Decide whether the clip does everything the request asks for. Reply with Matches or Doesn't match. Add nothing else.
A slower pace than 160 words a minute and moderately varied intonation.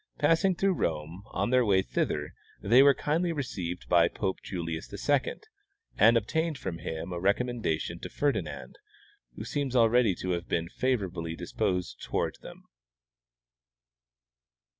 Doesn't match